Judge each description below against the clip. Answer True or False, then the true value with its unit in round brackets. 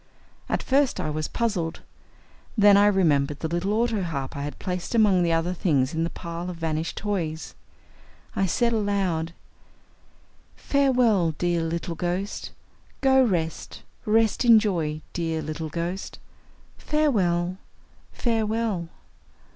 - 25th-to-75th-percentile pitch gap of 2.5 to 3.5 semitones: False (4.6 semitones)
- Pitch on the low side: False (180 Hz)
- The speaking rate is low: True (125 wpm)